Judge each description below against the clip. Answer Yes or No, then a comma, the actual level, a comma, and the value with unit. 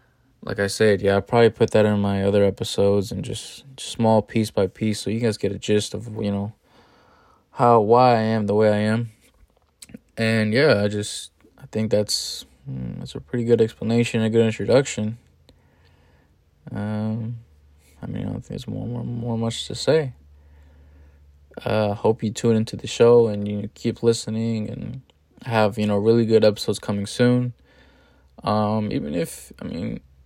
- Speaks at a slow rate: No, average, 180 wpm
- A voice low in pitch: Yes, low, 110 Hz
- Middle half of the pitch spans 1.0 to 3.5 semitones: Yes, narrow, 2.4 semitones